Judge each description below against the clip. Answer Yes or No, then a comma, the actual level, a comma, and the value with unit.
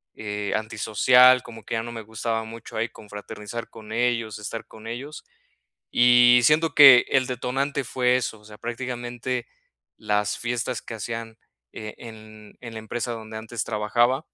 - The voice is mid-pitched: No, low, 115 Hz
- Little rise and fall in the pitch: Yes, narrow, 2.0 semitones